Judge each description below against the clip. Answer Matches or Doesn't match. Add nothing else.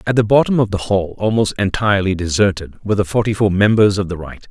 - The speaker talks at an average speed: Doesn't match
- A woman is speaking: Doesn't match